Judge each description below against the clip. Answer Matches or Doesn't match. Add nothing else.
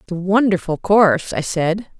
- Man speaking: Doesn't match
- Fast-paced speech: Doesn't match